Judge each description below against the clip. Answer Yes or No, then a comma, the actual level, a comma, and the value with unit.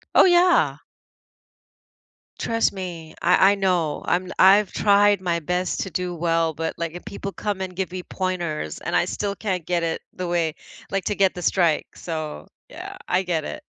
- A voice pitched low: No, medium, 180 Hz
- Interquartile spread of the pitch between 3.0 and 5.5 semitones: No, narrow, 2.6 semitones